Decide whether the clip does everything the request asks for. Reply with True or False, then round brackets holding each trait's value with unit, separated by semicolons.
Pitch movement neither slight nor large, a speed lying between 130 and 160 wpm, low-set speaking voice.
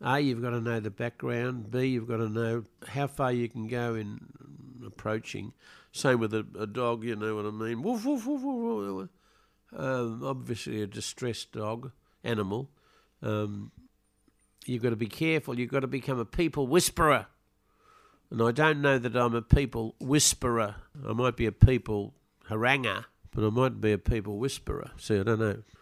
False (3.3 semitones; 185 wpm; 120 Hz)